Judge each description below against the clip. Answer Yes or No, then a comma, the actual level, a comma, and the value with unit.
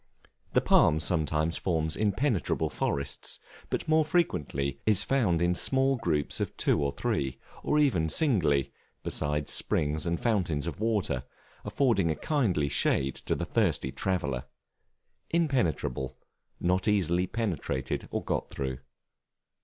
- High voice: No, very low, 85 Hz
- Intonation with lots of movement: Yes, wide, 7.5 semitones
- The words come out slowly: Yes, slow, 130 wpm